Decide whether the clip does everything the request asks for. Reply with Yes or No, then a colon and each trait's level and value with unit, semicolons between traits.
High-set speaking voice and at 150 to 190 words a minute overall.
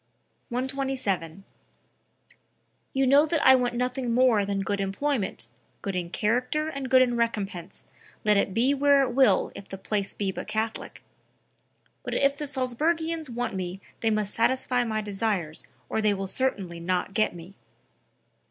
Yes: high, 230 Hz; average, 155 wpm